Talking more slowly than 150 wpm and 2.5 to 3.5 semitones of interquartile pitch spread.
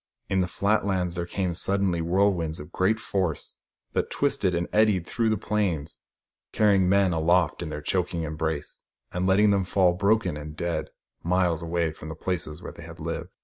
No: average, 185 wpm; average, 3.0 semitones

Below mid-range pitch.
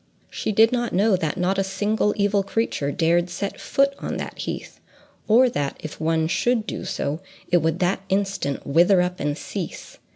No: high, 190 Hz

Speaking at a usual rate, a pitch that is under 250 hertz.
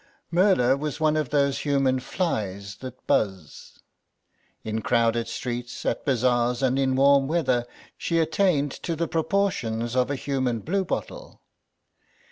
No: slow, 130 wpm; low, 135 Hz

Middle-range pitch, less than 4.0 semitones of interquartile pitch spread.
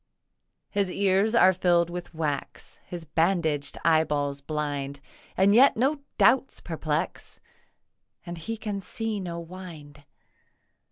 No: medium, 170 Hz; average, 4.5 semitones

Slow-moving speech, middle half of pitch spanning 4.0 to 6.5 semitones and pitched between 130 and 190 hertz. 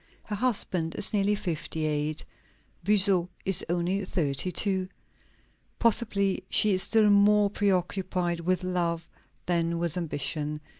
No: slow, 120 wpm; average, 3.2 semitones; medium, 185 Hz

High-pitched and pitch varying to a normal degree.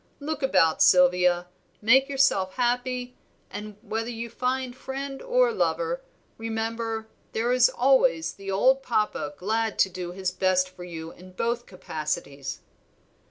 No: high, 225 Hz; wide, 5.7 semitones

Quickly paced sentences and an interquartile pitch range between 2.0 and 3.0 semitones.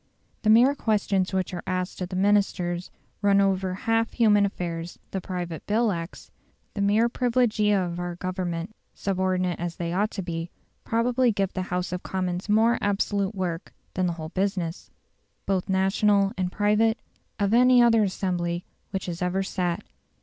No: average, 165 wpm; average, 2.7 semitones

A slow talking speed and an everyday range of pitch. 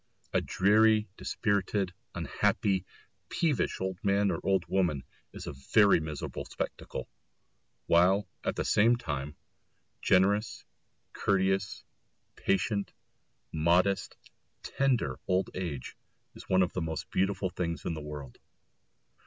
Yes: slow, 115 wpm; average, 3.3 semitones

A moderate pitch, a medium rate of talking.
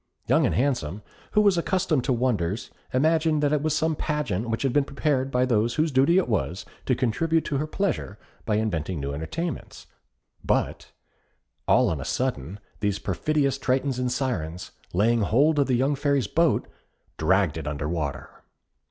No: low, 130 Hz; average, 170 wpm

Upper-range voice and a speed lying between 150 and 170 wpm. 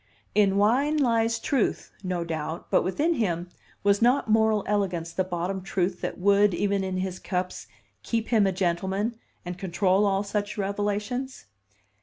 Yes: high, 200 Hz; average, 155 wpm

